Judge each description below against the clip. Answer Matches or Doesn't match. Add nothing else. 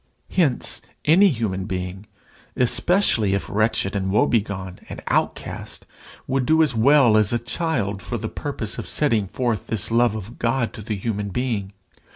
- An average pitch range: Matches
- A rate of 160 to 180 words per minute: Matches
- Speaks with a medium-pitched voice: Doesn't match